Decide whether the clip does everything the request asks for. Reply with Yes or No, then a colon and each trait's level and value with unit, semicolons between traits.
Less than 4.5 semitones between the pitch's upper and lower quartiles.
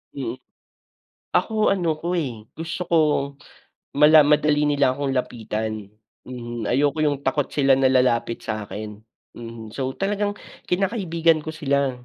No: average, 5.3 semitones